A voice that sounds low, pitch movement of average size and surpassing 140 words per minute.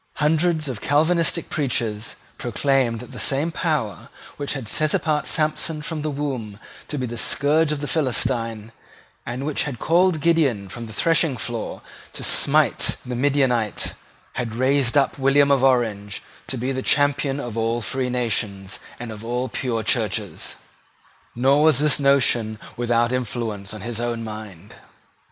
Yes: low, 130 Hz; average, 4.1 semitones; average, 155 wpm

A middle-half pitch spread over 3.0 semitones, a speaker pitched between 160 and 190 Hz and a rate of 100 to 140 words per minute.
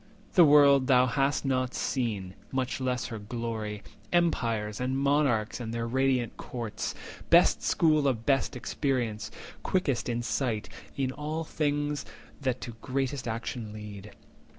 No: average, 3.4 semitones; low, 130 Hz; slow, 135 wpm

